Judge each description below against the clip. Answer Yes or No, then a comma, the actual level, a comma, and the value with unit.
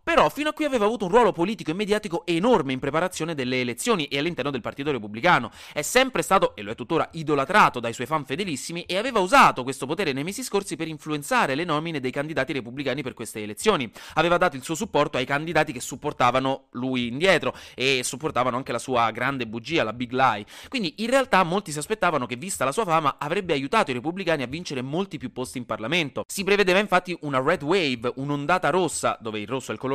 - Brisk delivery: Yes, fast, 215 wpm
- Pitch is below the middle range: No, medium, 150 Hz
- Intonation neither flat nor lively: No, wide, 5.9 semitones